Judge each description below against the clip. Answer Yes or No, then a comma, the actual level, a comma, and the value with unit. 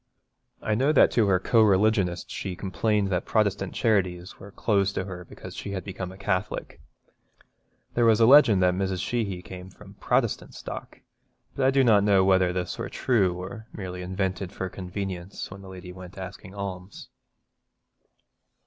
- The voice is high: No, very low, 95 Hz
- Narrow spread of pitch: Yes, narrow, 2.2 semitones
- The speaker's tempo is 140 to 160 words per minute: No, average, 175 wpm